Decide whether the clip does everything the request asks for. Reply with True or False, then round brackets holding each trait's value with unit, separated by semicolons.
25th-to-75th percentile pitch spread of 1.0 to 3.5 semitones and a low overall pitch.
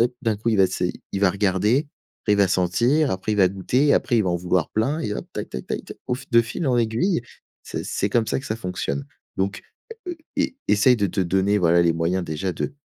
False (4.3 semitones; 100 Hz)